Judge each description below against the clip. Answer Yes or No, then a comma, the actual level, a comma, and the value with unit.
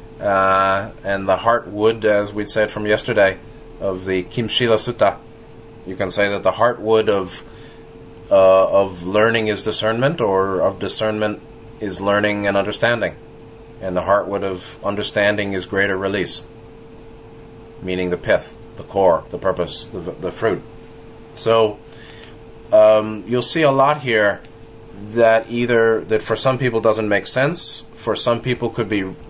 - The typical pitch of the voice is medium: No, low, 110 Hz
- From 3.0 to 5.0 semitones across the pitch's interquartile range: No, narrow, 2.4 semitones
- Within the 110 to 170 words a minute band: Yes, average, 145 wpm